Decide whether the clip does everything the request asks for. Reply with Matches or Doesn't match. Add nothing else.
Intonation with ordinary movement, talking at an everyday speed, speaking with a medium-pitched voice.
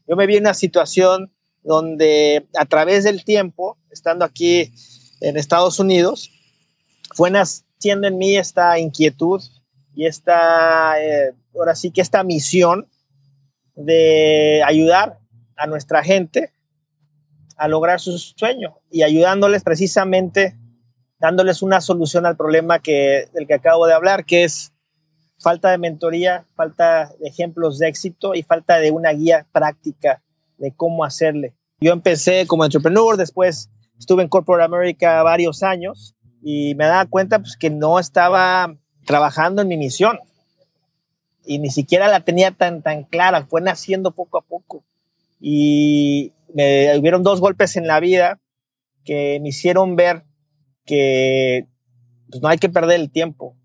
Matches